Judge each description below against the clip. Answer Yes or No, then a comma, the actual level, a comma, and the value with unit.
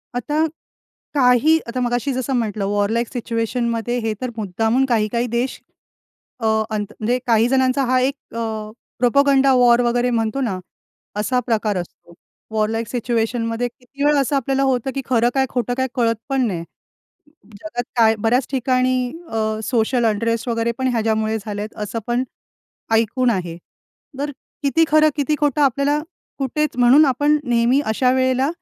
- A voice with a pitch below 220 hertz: No, high, 245 Hz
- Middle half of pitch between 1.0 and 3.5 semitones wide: Yes, average, 2.8 semitones